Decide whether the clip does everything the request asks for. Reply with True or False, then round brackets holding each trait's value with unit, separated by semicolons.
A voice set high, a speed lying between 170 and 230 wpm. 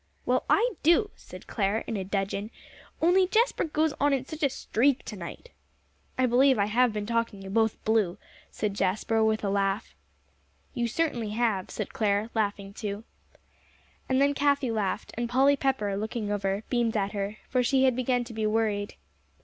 True (225 Hz; 180 wpm)